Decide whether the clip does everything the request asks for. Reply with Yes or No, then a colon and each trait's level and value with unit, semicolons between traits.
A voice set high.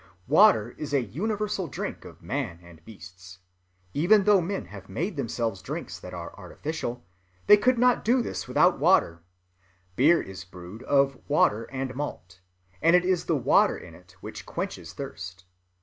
No: low, 135 Hz